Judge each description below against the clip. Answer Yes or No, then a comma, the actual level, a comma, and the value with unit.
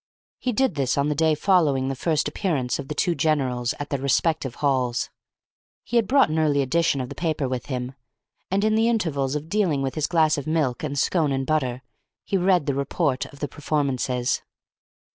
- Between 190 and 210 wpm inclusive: Yes, average, 200 wpm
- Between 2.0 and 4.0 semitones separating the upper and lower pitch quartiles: Yes, average, 3.7 semitones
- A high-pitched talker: No, medium, 145 Hz